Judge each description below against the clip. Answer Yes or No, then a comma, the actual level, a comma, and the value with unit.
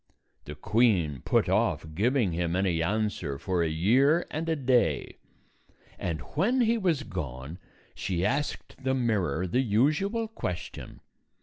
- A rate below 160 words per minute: Yes, slow, 135 wpm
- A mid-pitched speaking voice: No, low, 105 Hz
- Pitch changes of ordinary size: No, wide, 8.7 semitones